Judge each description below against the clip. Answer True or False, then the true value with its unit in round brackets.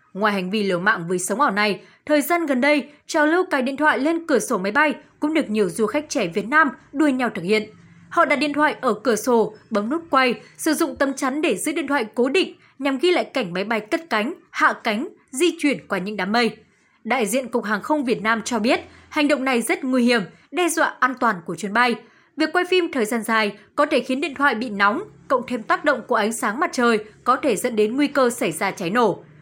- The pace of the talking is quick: True (255 wpm)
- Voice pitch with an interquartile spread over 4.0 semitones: True (5.6 semitones)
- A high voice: True (255 Hz)